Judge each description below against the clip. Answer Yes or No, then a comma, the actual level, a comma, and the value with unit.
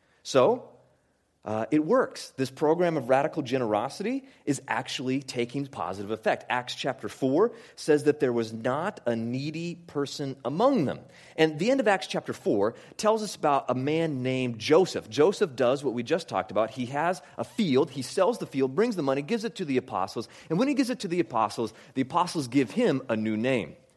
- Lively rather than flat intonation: Yes, wide, 6.0 semitones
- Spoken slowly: No, average, 200 wpm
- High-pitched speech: No, medium, 145 Hz